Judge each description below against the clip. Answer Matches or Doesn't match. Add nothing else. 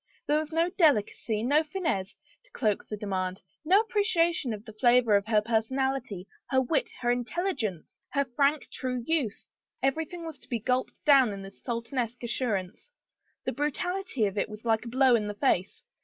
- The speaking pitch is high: Matches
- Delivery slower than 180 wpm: Doesn't match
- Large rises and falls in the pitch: Matches